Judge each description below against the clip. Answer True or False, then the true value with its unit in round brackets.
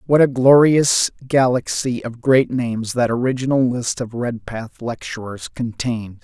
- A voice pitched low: True (125 Hz)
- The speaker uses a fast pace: False (135 wpm)